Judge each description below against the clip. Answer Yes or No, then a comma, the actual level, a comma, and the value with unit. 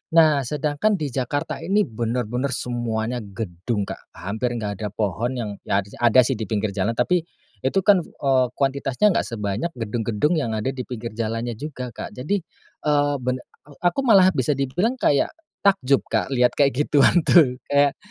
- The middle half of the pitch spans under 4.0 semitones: No, average, 4.4 semitones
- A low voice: Yes, low, 125 Hz